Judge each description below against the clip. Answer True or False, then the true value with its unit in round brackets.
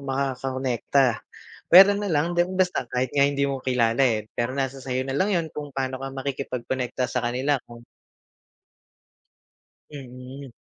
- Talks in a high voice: False (135 Hz)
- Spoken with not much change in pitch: True (1.8 semitones)